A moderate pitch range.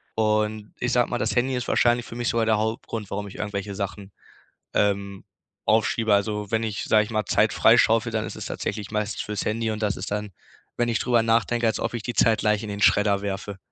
No: narrow, 1.8 semitones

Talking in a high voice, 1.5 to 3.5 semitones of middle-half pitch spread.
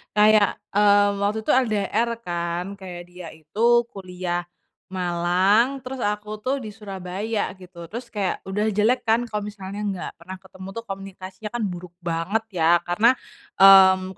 Yes: high, 195 Hz; average, 2.7 semitones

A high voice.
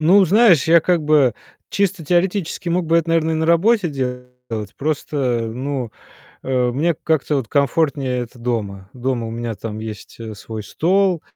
No: medium, 145 Hz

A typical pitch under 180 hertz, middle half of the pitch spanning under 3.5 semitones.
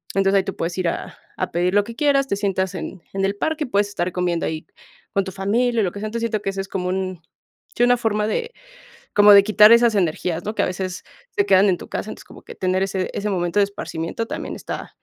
No: high, 195 Hz; average, 2.7 semitones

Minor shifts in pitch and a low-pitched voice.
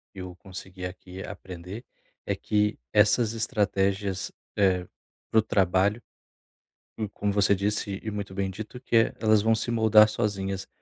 Yes: narrow, 2.2 semitones; low, 100 Hz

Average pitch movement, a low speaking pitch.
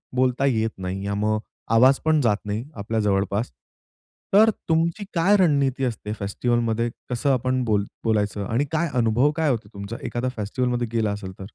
Yes: average, 4.4 semitones; low, 115 Hz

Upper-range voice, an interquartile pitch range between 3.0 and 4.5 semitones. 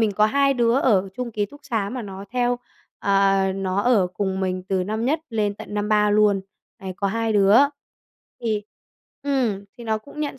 Yes: high, 210 Hz; average, 3.4 semitones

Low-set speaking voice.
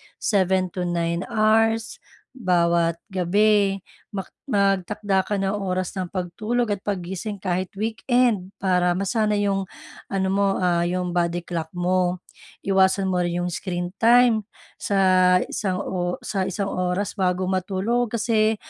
No: high, 190 Hz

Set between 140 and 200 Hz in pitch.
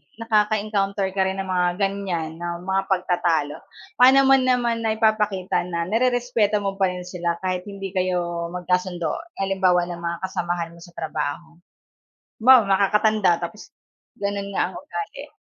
Yes: high, 190 Hz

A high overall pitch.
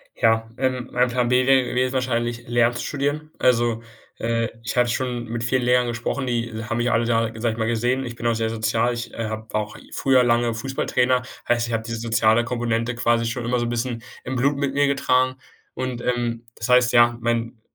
No: low, 120 Hz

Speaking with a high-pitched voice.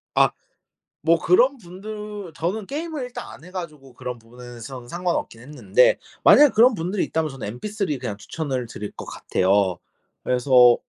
No: medium, 160 Hz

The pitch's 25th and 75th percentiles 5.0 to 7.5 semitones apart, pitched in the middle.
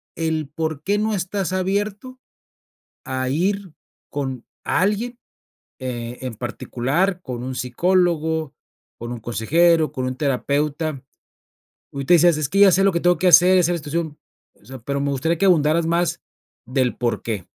Yes: wide, 5.5 semitones; medium, 160 Hz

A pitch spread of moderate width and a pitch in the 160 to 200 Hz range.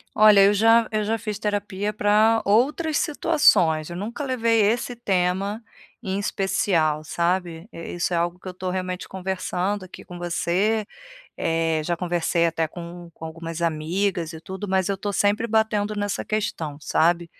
Yes: average, 3.6 semitones; high, 190 Hz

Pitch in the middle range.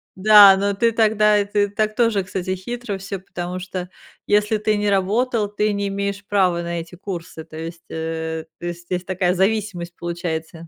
No: high, 195 Hz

